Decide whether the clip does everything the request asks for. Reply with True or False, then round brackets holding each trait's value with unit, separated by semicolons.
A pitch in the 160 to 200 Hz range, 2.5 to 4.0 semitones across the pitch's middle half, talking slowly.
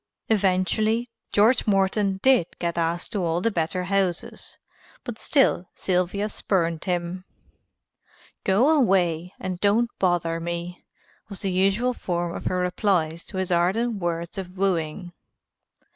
True (185 Hz; 2.9 semitones; 130 wpm)